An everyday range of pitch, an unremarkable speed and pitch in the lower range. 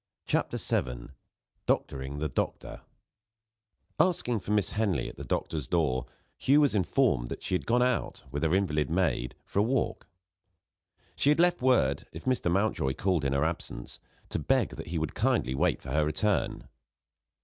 No: wide, 8.2 semitones; average, 170 wpm; very low, 85 Hz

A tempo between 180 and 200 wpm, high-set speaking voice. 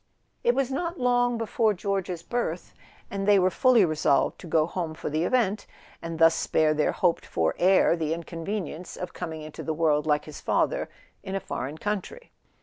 No: average, 185 wpm; medium, 180 Hz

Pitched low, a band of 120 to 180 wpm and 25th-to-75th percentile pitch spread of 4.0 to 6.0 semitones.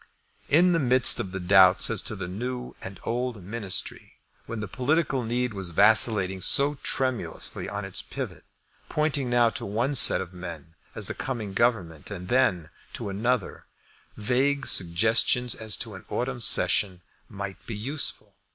Yes: low, 110 Hz; average, 160 wpm; average, 4.8 semitones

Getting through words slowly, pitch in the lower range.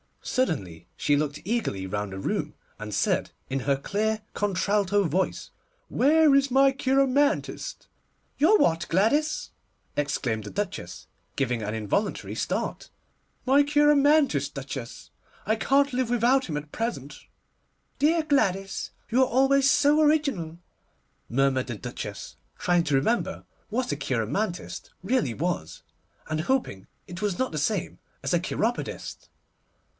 No: slow, 130 wpm; high, 200 Hz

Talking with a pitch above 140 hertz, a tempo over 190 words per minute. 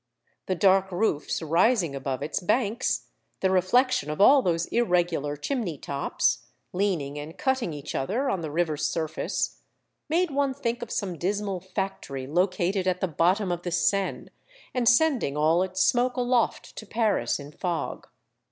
No: medium, 185 Hz; average, 155 wpm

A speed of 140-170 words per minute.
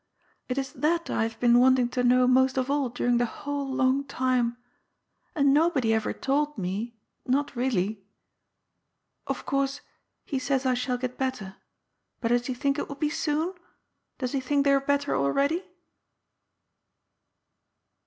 Yes: average, 160 wpm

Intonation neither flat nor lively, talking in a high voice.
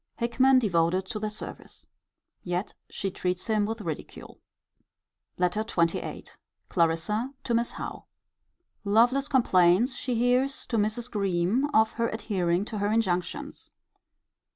Yes: average, 4.8 semitones; high, 215 Hz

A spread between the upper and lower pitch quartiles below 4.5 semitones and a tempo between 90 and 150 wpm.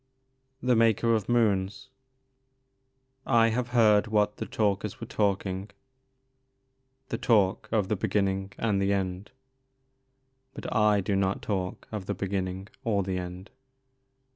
Yes: average, 2.9 semitones; slow, 135 wpm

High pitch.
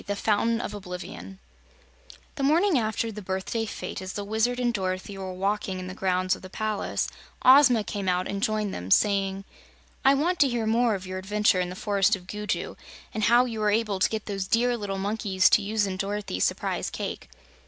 Yes: high, 205 Hz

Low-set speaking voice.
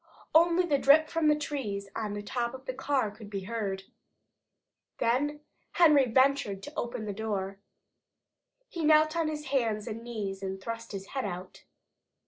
No: high, 235 Hz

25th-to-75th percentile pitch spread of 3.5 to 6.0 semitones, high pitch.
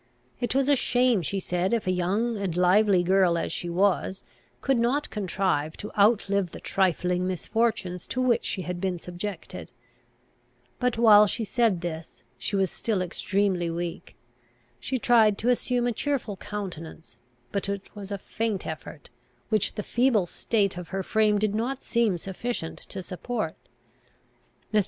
Yes: average, 4.1 semitones; high, 200 Hz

